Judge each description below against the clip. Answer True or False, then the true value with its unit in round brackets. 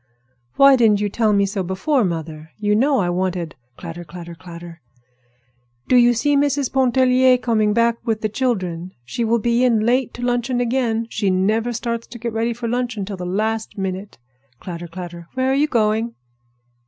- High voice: True (225 Hz)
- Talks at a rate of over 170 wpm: True (180 wpm)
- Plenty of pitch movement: False (4.7 semitones)